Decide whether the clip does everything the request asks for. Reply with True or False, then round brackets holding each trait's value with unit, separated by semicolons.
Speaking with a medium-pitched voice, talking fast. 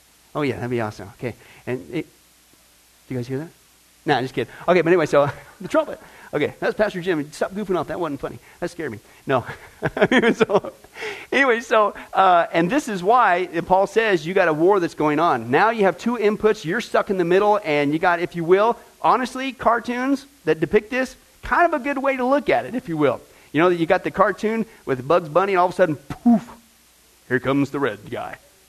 True (180 Hz; 225 wpm)